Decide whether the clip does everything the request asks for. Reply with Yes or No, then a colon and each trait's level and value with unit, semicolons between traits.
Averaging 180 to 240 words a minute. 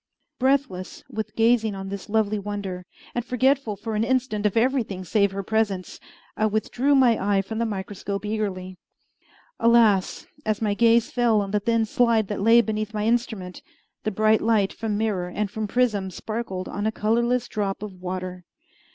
No: average, 170 wpm